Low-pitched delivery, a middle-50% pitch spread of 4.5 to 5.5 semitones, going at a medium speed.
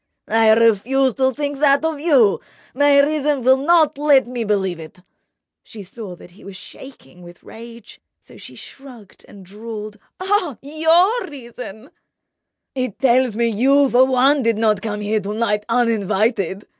No: high, 240 Hz; average, 5.1 semitones; average, 155 wpm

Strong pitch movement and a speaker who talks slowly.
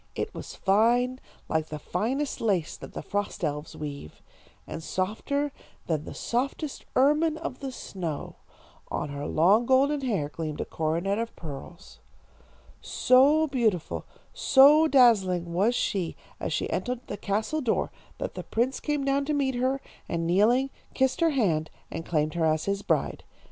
No: wide, 8.1 semitones; average, 160 wpm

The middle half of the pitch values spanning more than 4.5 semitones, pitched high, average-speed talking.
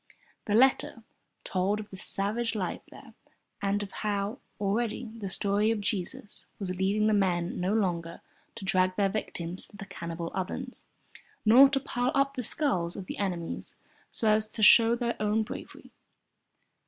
No: average, 3.2 semitones; high, 205 Hz; average, 165 wpm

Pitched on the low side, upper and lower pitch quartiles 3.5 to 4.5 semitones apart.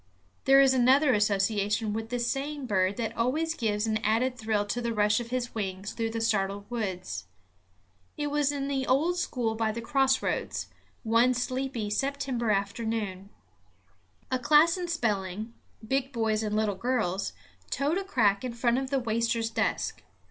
No: high, 230 Hz; average, 4.0 semitones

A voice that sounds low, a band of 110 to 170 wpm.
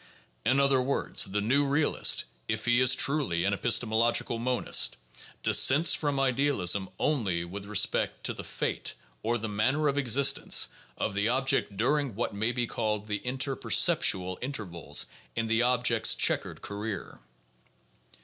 Yes: low, 120 Hz; average, 140 wpm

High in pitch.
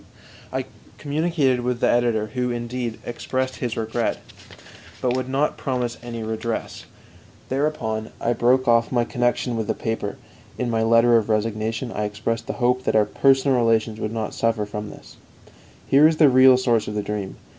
No: low, 120 Hz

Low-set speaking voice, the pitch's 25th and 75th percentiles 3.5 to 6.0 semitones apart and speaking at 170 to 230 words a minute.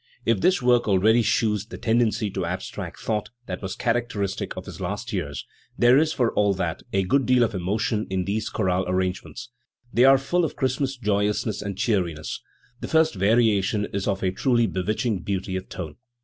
Yes: low, 105 Hz; average, 4.1 semitones; average, 190 wpm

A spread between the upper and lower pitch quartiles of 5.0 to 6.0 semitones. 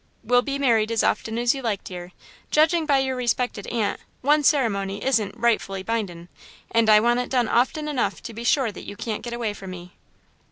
No: average, 4.0 semitones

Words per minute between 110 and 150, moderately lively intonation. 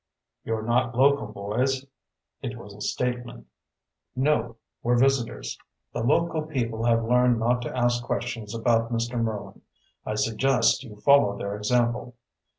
No: average, 140 wpm; narrow, 1.9 semitones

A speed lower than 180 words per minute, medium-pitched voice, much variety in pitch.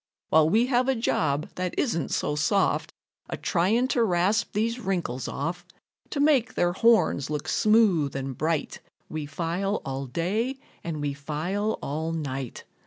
Yes: average, 155 wpm; medium, 175 Hz; wide, 6.7 semitones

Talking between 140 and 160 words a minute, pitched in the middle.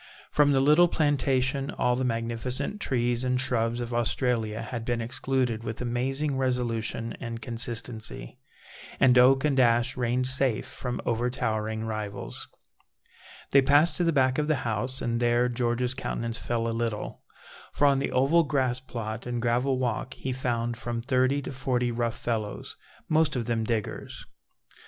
No: average, 155 wpm; low, 125 Hz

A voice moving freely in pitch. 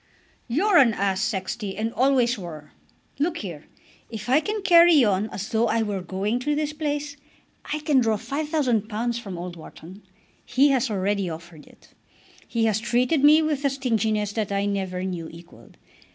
Yes: wide, 6.3 semitones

